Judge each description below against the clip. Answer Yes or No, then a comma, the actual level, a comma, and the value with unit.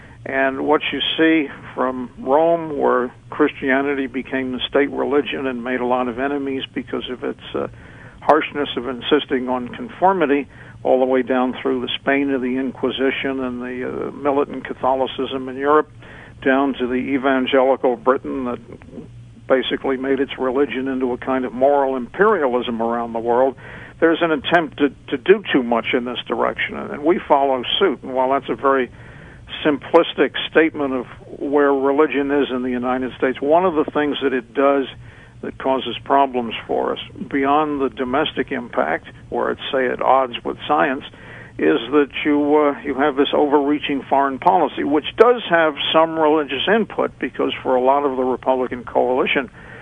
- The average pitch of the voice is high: No, low, 135 Hz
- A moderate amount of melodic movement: No, narrow, 2.1 semitones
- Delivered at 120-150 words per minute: No, average, 170 wpm